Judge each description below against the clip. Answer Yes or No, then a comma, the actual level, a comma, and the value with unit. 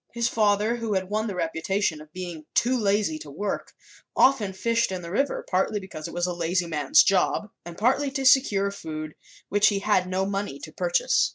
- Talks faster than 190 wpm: Yes, average, 200 wpm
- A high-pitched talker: Yes, high, 195 Hz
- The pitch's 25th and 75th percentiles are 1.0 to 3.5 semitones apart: No, average, 4.0 semitones